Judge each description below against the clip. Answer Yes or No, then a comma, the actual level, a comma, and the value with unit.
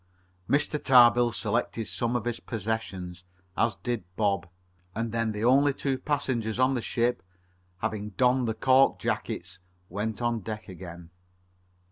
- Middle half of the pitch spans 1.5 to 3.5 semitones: Yes, average, 2.9 semitones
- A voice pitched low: Yes, low, 115 Hz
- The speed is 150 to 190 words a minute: No, average, 140 wpm